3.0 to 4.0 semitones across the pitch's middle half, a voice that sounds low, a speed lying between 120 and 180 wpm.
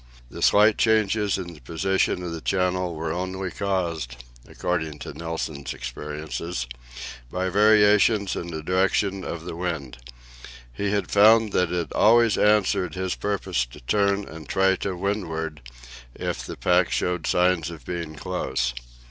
Yes: average, 3.5 semitones; very low, 90 Hz; average, 150 wpm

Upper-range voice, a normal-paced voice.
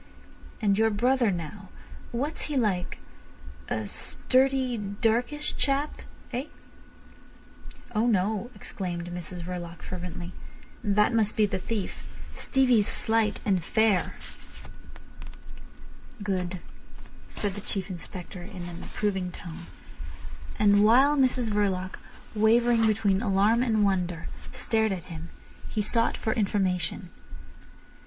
No: high, 205 Hz; slow, 105 wpm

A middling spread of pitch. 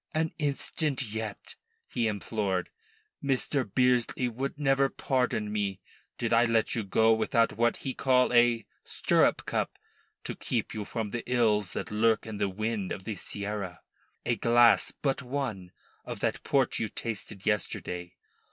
Yes: average, 3.3 semitones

